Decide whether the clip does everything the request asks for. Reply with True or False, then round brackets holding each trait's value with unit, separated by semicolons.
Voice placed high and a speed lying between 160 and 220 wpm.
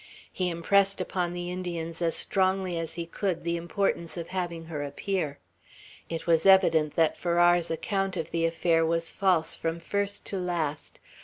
False (170 Hz; 165 wpm)